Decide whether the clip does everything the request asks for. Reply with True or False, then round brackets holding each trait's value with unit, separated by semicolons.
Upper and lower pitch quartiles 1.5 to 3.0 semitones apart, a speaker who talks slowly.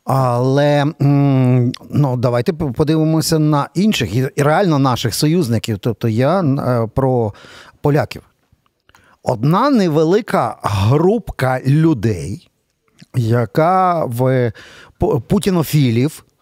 False (4.3 semitones; 75 wpm)